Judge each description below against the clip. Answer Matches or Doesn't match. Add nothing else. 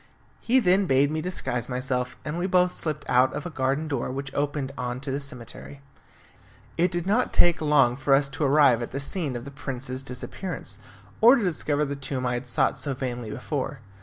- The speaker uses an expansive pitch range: Doesn't match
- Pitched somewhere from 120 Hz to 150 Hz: Matches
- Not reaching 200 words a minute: Doesn't match